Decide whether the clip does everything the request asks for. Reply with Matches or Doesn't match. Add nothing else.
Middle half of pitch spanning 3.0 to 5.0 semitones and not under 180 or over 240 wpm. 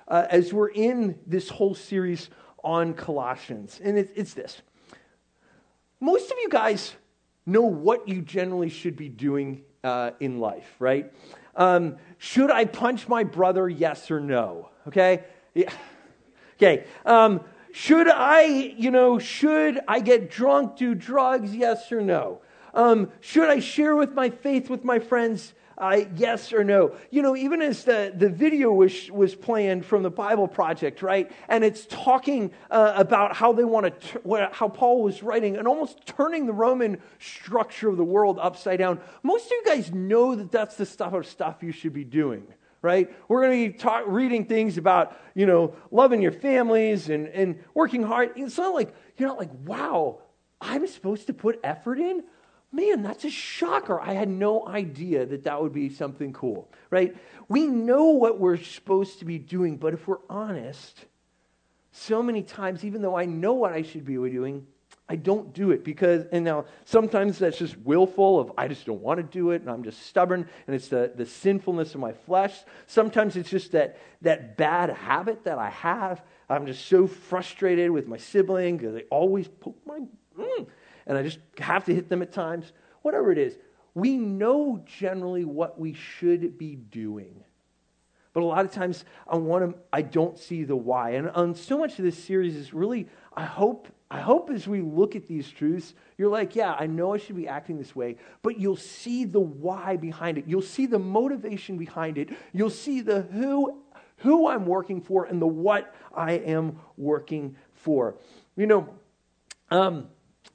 Doesn't match